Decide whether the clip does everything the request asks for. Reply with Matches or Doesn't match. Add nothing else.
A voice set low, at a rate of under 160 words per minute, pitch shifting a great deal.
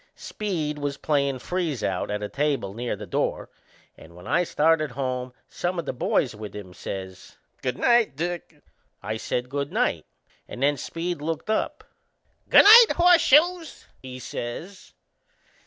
Doesn't match